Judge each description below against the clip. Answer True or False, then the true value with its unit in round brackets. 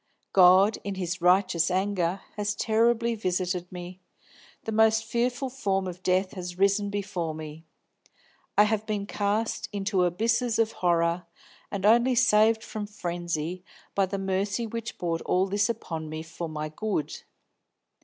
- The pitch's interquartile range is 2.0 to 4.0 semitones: True (3.5 semitones)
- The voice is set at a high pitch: True (195 Hz)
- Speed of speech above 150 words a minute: False (145 wpm)